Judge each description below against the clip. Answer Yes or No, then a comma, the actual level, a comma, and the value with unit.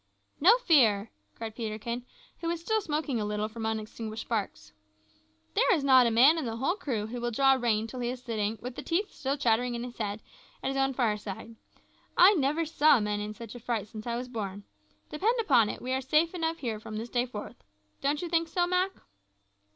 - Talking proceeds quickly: Yes, fast, 215 wpm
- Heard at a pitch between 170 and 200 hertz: No, high, 245 Hz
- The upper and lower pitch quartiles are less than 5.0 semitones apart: No, wide, 5.4 semitones